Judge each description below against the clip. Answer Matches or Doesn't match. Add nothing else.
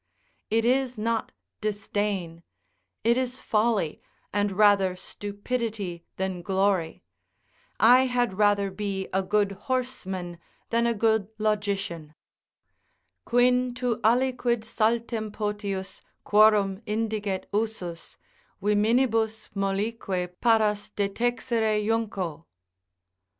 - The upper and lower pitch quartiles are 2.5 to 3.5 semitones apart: Matches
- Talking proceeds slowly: Matches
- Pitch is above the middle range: Matches